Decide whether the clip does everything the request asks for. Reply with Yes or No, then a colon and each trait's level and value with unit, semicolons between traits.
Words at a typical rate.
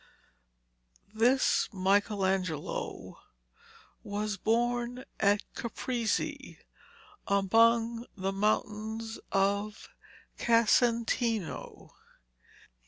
No: slow, 50 wpm